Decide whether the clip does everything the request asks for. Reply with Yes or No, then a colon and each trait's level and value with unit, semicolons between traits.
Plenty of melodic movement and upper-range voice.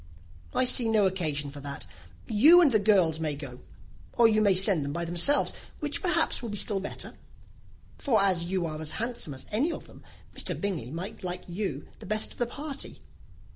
Yes: wide, 6.0 semitones; high, 195 Hz